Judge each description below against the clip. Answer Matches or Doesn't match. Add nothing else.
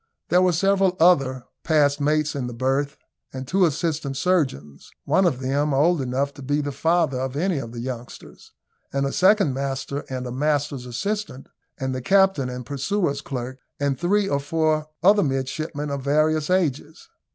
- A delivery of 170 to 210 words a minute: Matches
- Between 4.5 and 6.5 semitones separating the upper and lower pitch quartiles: Doesn't match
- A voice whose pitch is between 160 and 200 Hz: Doesn't match